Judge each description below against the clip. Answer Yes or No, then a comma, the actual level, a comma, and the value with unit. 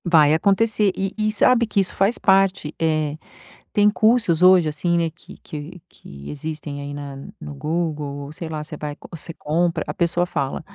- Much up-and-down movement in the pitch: No, average, 4.4 semitones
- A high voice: No, medium, 165 Hz